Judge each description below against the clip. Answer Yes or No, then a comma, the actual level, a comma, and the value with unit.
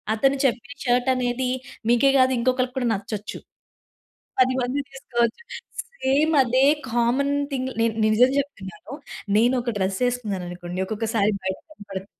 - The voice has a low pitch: No, high, 245 Hz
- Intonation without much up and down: No, average, 3.5 semitones